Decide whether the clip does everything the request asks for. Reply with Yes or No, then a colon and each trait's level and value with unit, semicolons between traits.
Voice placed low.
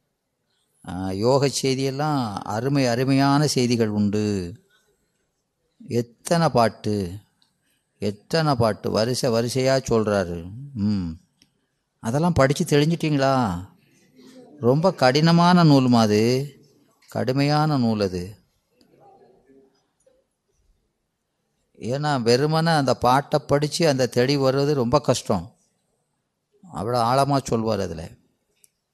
Yes: low, 130 Hz